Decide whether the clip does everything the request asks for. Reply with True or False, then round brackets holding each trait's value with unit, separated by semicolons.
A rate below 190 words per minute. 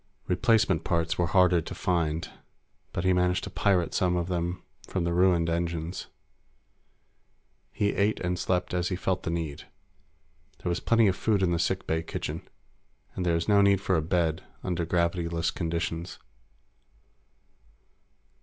True (160 wpm)